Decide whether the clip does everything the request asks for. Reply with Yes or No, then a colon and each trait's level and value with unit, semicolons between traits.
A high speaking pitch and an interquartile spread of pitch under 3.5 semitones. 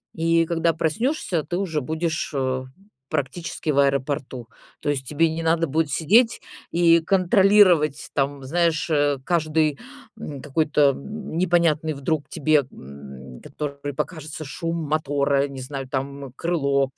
No: medium, 155 Hz; average, 3.1 semitones